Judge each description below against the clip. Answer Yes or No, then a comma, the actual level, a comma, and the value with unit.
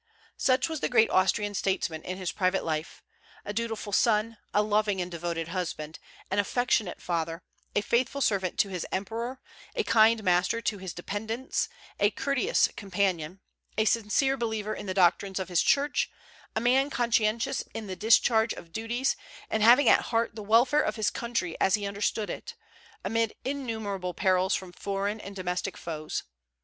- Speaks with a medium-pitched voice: No, high, 210 Hz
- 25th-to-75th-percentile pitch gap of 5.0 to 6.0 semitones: No, average, 3.7 semitones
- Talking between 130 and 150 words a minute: No, average, 165 wpm